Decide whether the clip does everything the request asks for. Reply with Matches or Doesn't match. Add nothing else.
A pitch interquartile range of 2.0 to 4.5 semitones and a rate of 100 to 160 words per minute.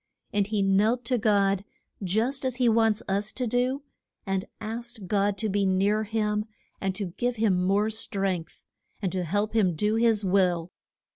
Doesn't match